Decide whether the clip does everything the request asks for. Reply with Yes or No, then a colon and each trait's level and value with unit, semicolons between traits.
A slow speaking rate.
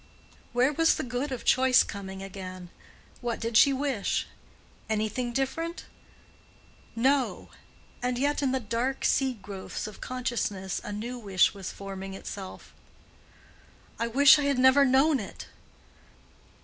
Yes: slow, 130 wpm